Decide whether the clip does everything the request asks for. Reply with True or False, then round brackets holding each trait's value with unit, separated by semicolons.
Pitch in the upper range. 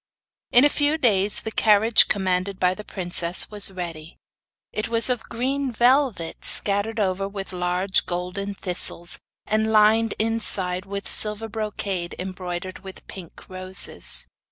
True (200 Hz)